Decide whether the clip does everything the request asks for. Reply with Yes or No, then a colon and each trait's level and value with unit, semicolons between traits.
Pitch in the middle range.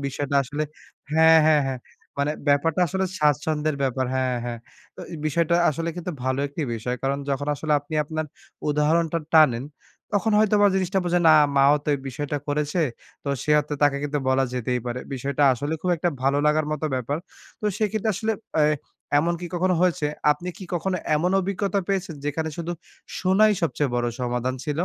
Yes: medium, 150 Hz